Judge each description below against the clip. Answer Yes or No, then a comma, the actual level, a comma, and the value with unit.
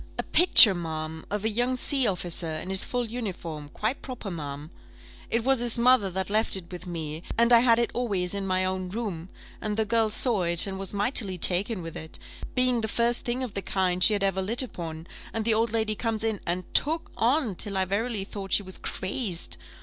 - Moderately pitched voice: No, high, 200 Hz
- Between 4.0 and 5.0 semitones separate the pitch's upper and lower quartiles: Yes, average, 4.4 semitones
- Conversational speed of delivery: No, fast, 220 wpm